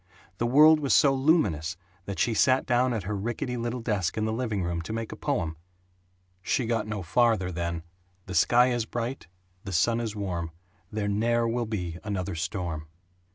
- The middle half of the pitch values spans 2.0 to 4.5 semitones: No, average, 4.9 semitones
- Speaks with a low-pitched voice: Yes, low, 110 Hz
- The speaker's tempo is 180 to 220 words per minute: Yes, average, 185 wpm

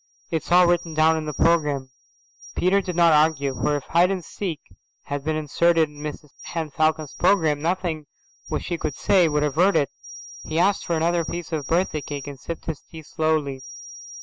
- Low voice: No, medium, 160 Hz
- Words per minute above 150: Yes, average, 190 wpm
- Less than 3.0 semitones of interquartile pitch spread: Yes, narrow, 2.5 semitones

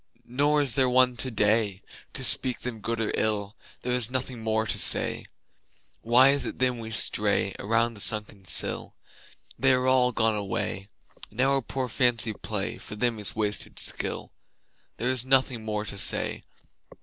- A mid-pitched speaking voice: No, low, 115 Hz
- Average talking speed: Yes, average, 170 wpm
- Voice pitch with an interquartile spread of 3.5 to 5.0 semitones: No, average, 3.1 semitones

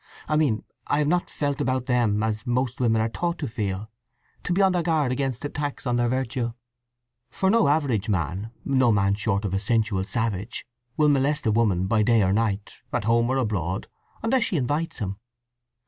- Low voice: Yes, low, 120 Hz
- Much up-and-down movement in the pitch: No, average, 5.0 semitones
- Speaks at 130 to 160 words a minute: No, average, 185 wpm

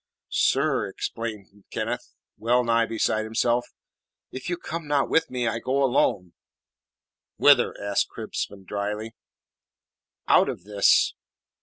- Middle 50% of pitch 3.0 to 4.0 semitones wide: Yes, average, 3.7 semitones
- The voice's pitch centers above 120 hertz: No, low, 115 Hz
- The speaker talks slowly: Yes, slow, 120 wpm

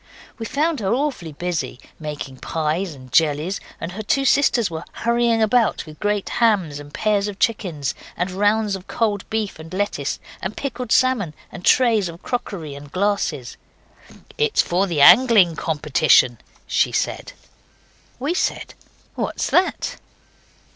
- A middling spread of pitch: No, wide, 6.3 semitones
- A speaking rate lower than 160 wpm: Yes, average, 145 wpm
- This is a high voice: Yes, high, 195 Hz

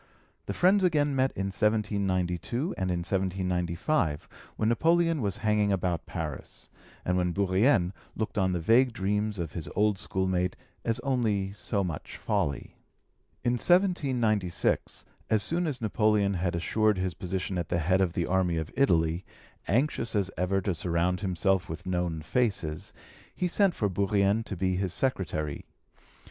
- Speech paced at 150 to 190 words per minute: Yes, average, 155 wpm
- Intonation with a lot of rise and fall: No, average, 3.9 semitones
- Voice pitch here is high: No, very low, 95 Hz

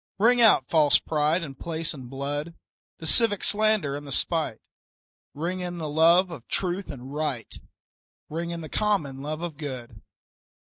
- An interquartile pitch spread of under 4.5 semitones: Yes, average, 3.7 semitones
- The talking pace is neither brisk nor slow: Yes, average, 160 wpm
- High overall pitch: No, medium, 160 Hz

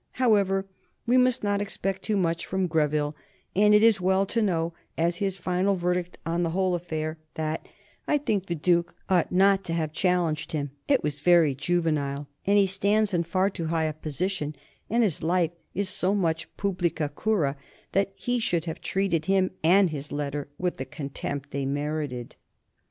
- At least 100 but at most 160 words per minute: No, average, 180 wpm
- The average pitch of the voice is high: No, medium, 175 Hz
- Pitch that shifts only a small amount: No, average, 3.9 semitones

